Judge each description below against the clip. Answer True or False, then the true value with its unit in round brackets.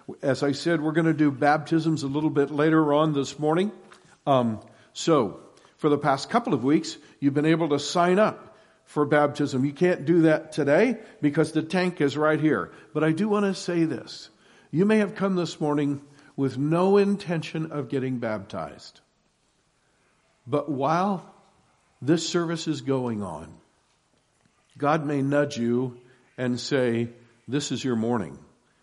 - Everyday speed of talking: True (160 wpm)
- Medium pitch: True (150 Hz)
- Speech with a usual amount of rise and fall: True (3.5 semitones)